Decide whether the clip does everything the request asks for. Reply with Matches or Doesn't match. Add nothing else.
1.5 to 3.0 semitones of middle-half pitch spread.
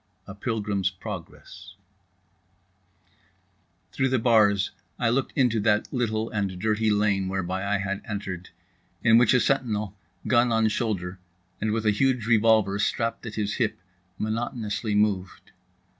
Matches